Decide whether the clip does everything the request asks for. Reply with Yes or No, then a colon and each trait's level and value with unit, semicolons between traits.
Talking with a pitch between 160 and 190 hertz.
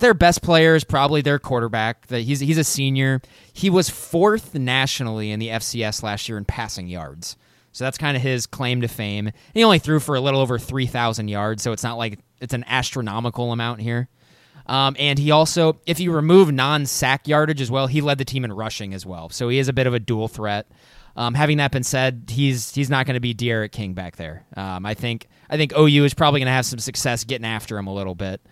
No: low, 130 Hz